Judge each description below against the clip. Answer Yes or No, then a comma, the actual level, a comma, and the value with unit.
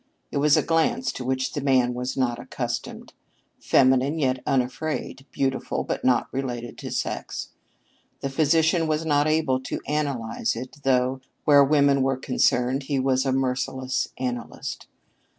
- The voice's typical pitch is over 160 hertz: No, low, 135 Hz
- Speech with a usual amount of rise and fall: No, narrow, 2.2 semitones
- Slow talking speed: No, average, 150 wpm